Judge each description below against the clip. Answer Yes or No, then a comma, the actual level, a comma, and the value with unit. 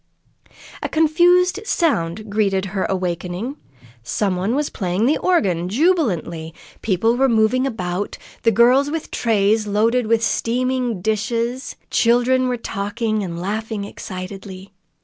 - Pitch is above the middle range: Yes, high, 220 Hz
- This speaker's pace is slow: Yes, slow, 120 wpm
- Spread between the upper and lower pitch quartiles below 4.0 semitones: No, average, 4.9 semitones